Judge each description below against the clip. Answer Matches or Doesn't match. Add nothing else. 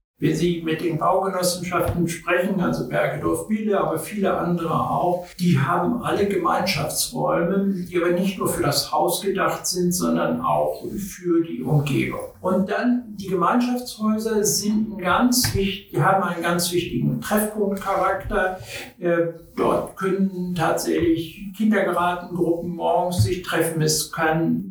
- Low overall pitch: Doesn't match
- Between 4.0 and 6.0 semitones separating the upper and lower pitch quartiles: Doesn't match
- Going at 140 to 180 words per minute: Doesn't match